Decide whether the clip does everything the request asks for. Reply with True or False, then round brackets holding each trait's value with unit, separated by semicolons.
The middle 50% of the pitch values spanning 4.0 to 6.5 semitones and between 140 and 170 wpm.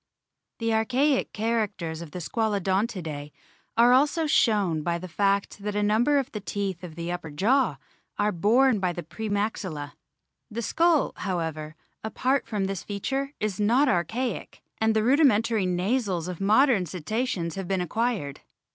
True (4.8 semitones; 155 wpm)